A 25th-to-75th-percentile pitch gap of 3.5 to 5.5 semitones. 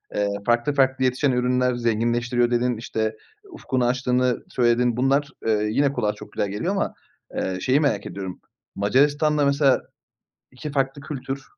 No: average, 2.7 semitones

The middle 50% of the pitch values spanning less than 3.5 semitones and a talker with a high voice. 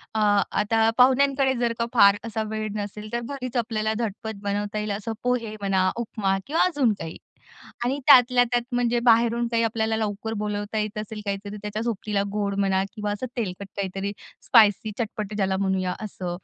Yes: narrow, 2.6 semitones; high, 215 Hz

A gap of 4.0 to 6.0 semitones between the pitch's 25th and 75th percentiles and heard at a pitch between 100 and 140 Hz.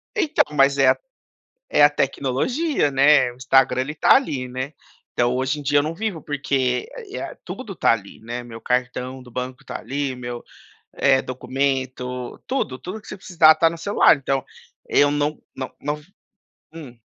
No: average, 3.0 semitones; low, 135 Hz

